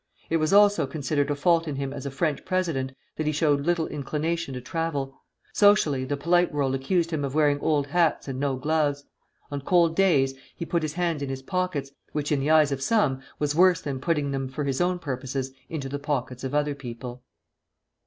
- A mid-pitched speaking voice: Yes, medium, 145 Hz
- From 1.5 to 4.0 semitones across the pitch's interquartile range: Yes, average, 3.4 semitones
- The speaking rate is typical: No, fast, 210 wpm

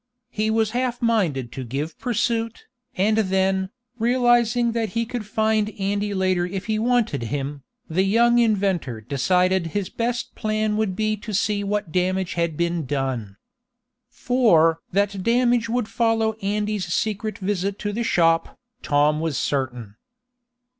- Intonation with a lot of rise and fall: No, average, 4.8 semitones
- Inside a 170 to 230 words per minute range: No, average, 145 wpm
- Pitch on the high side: Yes, high, 200 Hz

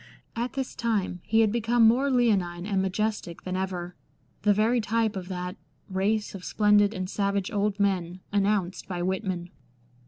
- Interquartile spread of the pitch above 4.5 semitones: No, average, 3.0 semitones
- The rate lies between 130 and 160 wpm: No, average, 180 wpm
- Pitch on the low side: No, high, 200 Hz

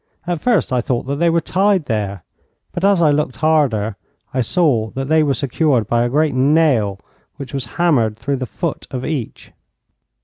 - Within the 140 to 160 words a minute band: No, average, 190 wpm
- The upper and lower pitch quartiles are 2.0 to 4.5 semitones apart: No, average, 5.1 semitones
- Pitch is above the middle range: No, medium, 140 Hz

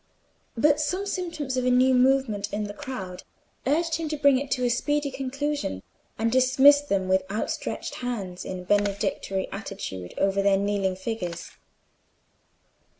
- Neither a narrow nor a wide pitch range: No, wide, 6.2 semitones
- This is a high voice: Yes, very high, 250 Hz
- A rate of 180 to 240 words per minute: No, average, 150 wpm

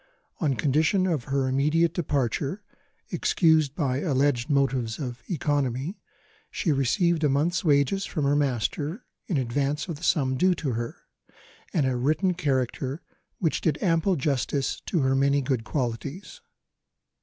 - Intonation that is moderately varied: Yes, average, 3.7 semitones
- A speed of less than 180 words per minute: Yes, average, 145 wpm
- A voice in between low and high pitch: Yes, medium, 145 Hz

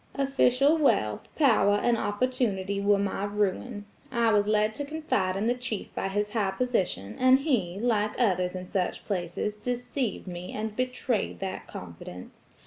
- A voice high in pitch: Yes, high, 210 Hz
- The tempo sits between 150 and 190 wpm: Yes, average, 155 wpm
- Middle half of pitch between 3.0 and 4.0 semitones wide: No, average, 4.5 semitones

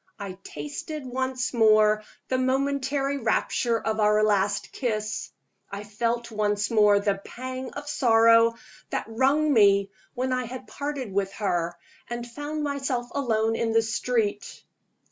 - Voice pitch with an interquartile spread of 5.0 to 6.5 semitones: No, average, 3.7 semitones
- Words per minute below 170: Yes, average, 140 wpm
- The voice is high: Yes, high, 230 Hz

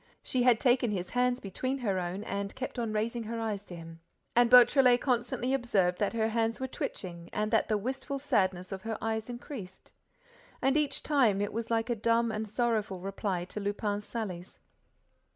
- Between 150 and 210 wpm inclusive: Yes, average, 190 wpm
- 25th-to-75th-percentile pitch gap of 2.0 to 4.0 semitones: Yes, average, 3.6 semitones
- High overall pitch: Yes, high, 220 Hz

